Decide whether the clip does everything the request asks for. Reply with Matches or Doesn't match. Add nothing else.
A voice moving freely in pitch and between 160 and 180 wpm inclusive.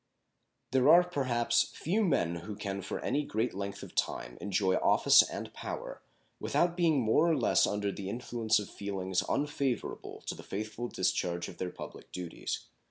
Matches